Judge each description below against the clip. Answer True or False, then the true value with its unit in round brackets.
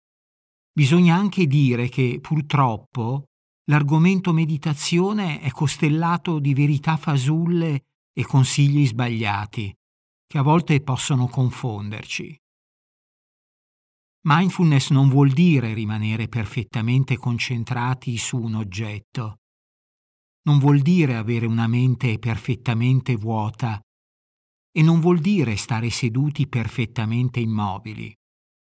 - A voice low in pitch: True (130 Hz)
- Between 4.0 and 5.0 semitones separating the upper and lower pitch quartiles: True (4.7 semitones)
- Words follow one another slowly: True (95 wpm)